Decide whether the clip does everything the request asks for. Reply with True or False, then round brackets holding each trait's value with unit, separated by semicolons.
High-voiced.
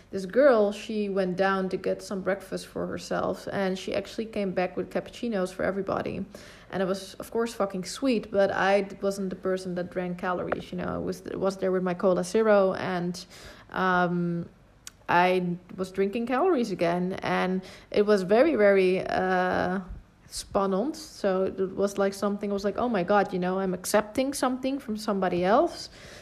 True (195 Hz)